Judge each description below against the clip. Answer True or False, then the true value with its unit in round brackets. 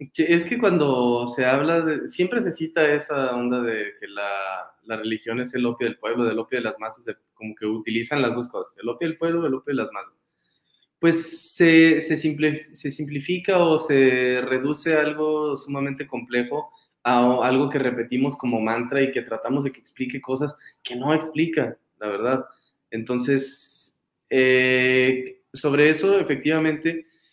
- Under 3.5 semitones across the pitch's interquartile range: False (4.0 semitones)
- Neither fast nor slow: True (165 wpm)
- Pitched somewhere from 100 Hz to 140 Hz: True (135 Hz)